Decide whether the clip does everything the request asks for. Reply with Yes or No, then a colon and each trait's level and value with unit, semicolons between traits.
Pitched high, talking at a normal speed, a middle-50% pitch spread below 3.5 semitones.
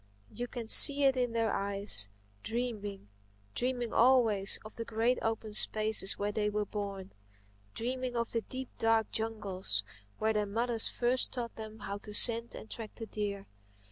Yes: high, 220 Hz; average, 160 wpm; average, 2.7 semitones